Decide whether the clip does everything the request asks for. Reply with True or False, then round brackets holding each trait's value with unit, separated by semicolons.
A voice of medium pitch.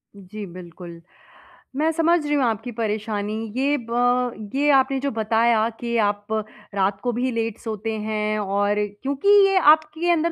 False (230 Hz)